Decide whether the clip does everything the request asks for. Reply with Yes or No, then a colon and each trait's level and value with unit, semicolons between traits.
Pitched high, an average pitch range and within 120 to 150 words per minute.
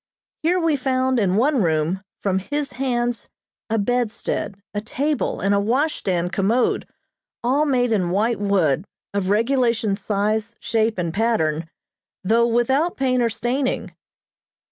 Yes: high, 230 Hz; average, 4.4 semitones; slow, 135 wpm